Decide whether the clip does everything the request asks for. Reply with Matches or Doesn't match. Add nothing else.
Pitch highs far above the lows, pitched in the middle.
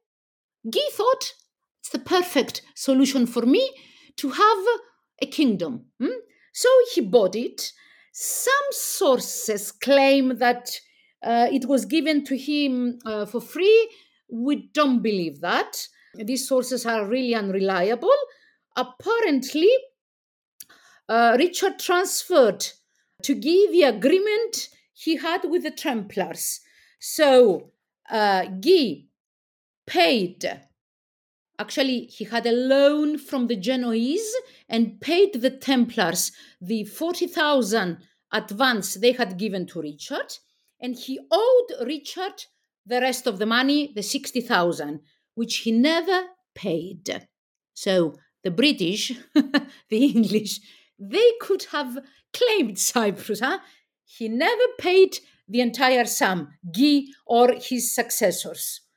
Doesn't match